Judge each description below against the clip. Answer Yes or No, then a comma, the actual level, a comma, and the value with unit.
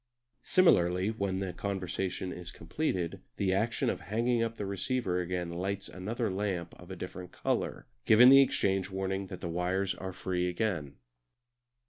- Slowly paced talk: No, average, 155 wpm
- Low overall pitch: Yes, very low, 95 Hz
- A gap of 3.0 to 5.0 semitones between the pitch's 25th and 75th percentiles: No, narrow, 2.6 semitones